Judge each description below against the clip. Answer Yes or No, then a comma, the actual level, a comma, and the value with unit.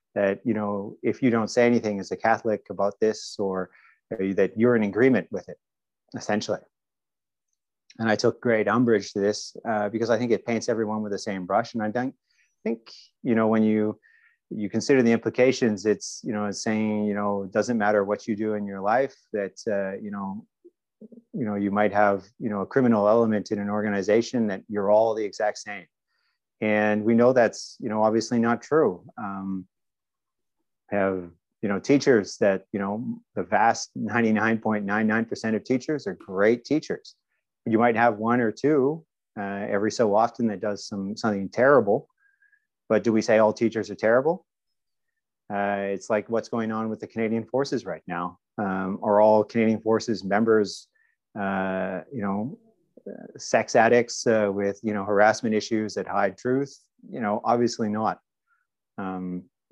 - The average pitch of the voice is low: Yes, low, 110 Hz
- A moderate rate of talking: Yes, average, 175 wpm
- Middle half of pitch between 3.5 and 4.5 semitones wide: No, narrow, 2.6 semitones